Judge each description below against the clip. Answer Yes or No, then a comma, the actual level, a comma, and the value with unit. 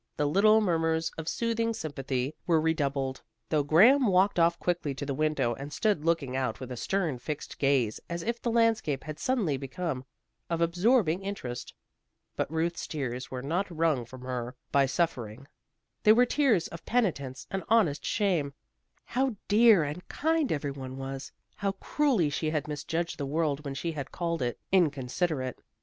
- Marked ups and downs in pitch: Yes, wide, 5.9 semitones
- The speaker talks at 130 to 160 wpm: No, average, 170 wpm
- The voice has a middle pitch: Yes, medium, 160 Hz